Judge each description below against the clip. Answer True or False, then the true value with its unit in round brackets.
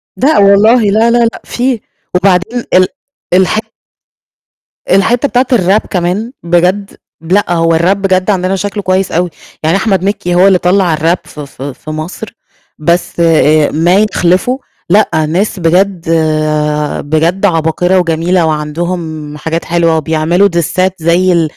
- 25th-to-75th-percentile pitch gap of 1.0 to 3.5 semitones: True (3.2 semitones)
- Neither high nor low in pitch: True (180 Hz)